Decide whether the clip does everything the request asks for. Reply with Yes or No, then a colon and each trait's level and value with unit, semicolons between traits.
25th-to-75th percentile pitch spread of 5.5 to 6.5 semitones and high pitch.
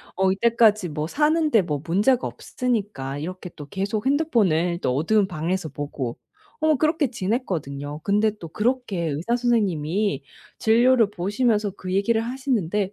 Yes: wide, 6.1 semitones; high, 200 Hz